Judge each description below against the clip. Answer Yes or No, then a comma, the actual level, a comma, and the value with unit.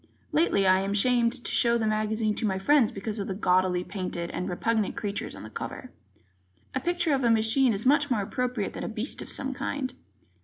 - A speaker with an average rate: No, fast, 215 wpm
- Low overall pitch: No, high, 220 Hz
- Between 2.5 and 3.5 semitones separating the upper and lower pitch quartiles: No, average, 4.6 semitones